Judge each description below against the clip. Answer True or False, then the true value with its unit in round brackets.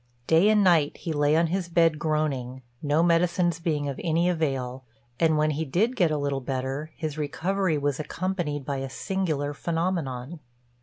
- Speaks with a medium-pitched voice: True (155 Hz)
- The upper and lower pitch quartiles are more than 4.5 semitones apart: False (3.2 semitones)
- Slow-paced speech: False (170 wpm)